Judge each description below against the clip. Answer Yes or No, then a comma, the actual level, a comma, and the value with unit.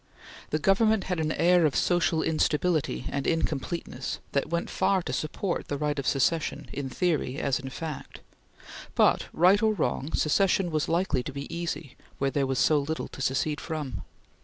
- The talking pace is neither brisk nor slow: Yes, average, 175 wpm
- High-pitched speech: No, medium, 155 Hz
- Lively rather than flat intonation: No, average, 3.8 semitones